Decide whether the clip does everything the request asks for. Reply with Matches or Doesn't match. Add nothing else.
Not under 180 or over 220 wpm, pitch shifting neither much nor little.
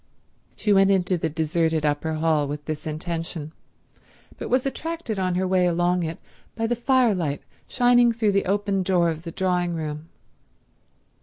Doesn't match